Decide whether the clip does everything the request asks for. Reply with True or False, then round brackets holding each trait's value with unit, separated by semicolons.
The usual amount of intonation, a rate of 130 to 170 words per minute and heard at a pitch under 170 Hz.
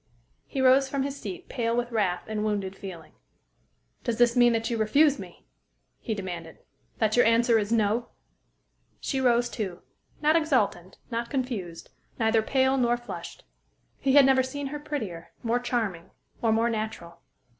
False (3.8 semitones; 160 wpm; 235 Hz)